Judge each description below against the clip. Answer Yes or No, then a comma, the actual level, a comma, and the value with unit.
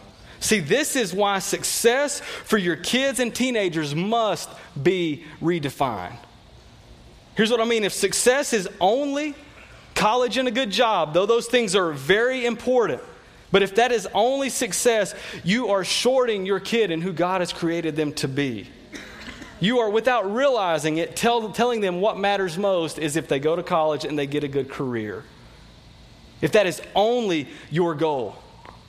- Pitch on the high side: Yes, high, 200 Hz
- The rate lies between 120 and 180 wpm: Yes, average, 165 wpm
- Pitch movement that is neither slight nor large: No, wide, 6.5 semitones